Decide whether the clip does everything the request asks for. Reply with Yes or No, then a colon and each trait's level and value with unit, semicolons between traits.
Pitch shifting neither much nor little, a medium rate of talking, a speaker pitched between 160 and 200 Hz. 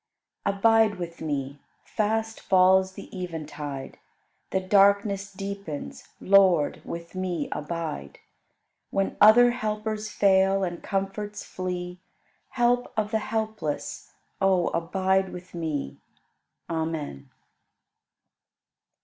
No: average, 3.7 semitones; slow, 100 wpm; high, 190 Hz